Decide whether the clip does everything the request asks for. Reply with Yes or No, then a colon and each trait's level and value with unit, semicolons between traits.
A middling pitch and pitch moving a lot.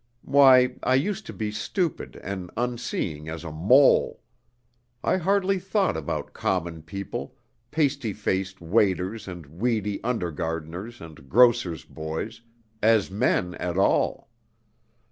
No: low, 105 Hz; wide, 6.5 semitones